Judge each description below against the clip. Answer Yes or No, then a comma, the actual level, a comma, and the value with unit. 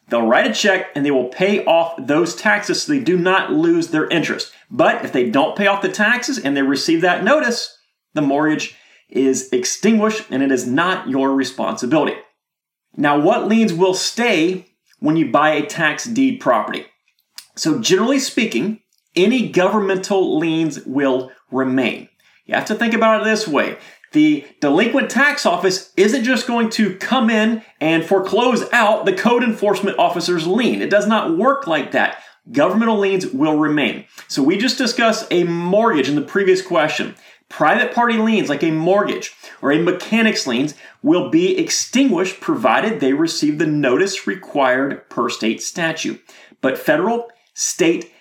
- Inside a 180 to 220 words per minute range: No, average, 165 wpm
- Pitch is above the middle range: Yes, high, 205 Hz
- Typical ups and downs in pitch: No, wide, 5.9 semitones